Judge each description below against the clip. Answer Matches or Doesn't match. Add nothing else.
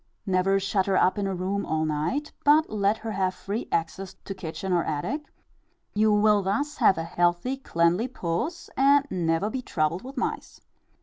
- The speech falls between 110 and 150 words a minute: Doesn't match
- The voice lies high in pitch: Matches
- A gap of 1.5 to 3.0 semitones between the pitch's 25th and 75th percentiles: Doesn't match